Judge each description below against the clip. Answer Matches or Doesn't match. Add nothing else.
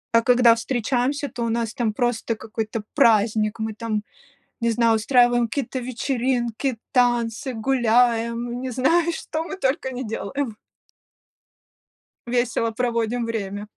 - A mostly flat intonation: Matches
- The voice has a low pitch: Doesn't match